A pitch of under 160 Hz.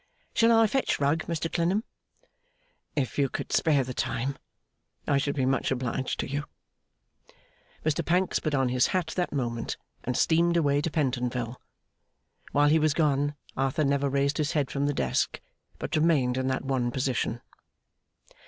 Yes: medium, 140 Hz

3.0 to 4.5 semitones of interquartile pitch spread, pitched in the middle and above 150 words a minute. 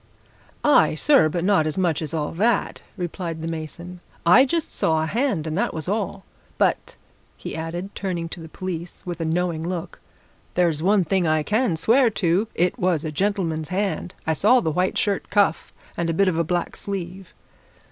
Yes: average, 3.5 semitones; medium, 175 Hz; average, 190 wpm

